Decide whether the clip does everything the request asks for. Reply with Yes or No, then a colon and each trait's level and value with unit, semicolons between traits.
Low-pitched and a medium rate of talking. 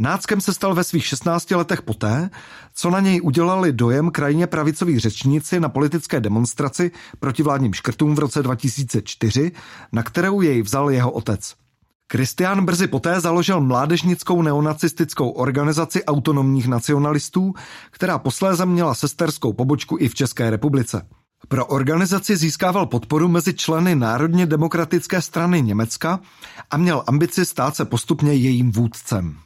No: medium, 150 Hz; average, 135 wpm